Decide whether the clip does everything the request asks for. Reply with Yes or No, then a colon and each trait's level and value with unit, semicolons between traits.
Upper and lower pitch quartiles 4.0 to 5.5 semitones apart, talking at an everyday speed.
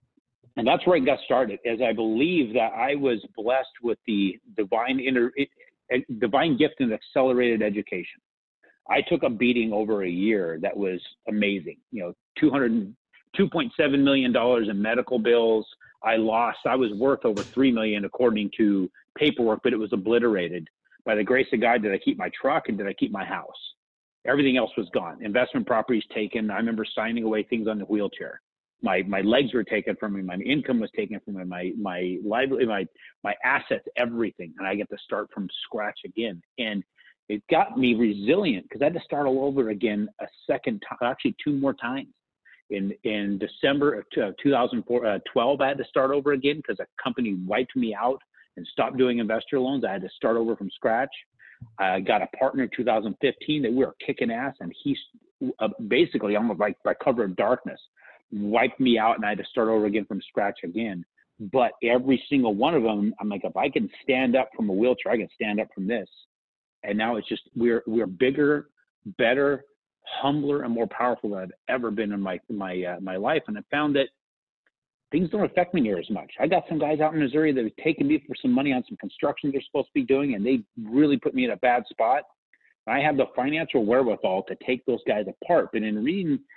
No: average, 5.1 semitones; fast, 210 wpm